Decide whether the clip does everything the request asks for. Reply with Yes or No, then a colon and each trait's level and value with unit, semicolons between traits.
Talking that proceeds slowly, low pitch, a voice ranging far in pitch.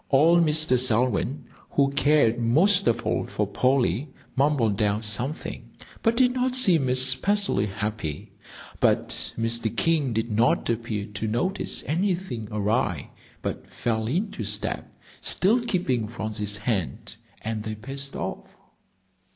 Yes: slow, 125 wpm; low, 125 Hz; wide, 6.2 semitones